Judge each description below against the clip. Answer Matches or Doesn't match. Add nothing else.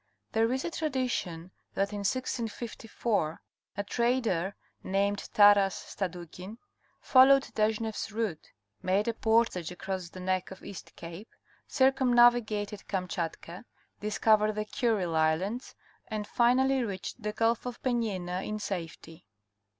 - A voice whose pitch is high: Matches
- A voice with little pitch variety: Doesn't match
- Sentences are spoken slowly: Matches